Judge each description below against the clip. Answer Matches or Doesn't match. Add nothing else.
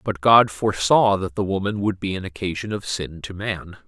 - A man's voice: Matches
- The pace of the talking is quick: Matches